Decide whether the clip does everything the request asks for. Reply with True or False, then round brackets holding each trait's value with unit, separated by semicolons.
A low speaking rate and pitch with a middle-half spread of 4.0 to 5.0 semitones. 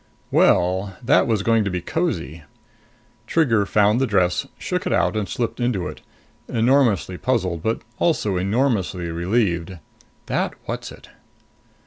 True (130 wpm; 4.6 semitones)